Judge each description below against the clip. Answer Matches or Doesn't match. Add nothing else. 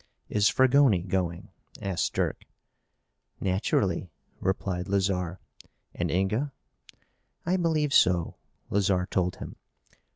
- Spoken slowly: Matches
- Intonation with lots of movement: Doesn't match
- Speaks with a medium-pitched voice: Doesn't match